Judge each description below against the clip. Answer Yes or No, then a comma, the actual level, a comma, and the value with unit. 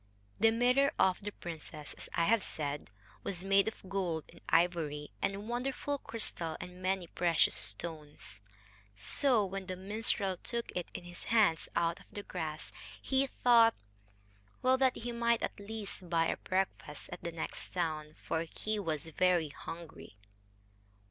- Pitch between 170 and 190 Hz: Yes, medium, 185 Hz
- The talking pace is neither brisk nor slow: Yes, average, 155 wpm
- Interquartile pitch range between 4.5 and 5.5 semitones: Yes, average, 5.2 semitones